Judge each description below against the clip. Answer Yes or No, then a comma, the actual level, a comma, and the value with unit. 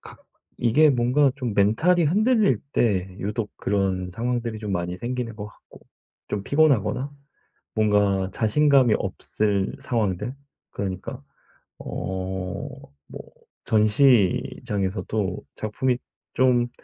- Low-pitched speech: Yes, low, 110 Hz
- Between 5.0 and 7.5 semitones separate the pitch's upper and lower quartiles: No, average, 4.5 semitones